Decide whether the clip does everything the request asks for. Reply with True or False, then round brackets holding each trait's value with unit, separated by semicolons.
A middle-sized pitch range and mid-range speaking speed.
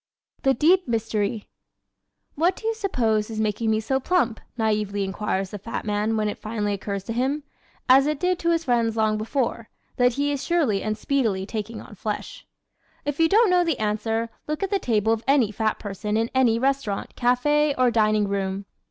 True (4.8 semitones; 195 wpm)